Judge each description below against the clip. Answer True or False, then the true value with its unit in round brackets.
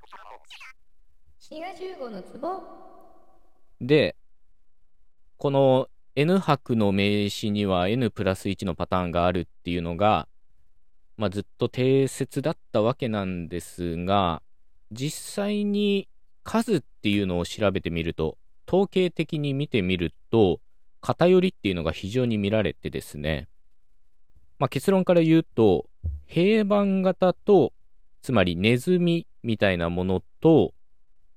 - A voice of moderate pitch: False (105 Hz)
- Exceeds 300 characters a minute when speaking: False (210 characters per minute)